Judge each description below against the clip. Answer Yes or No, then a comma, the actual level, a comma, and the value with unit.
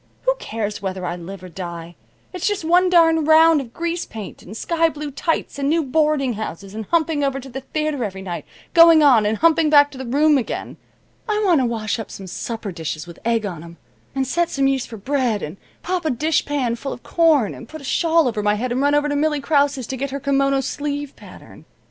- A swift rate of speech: Yes, fast, 230 wpm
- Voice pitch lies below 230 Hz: No, very high, 275 Hz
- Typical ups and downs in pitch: No, wide, 6.2 semitones